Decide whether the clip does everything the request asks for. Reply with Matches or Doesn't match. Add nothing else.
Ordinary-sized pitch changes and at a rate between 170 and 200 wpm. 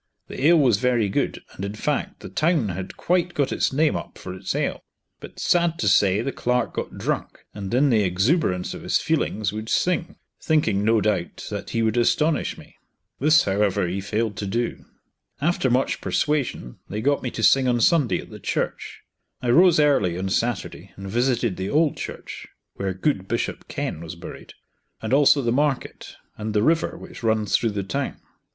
Doesn't match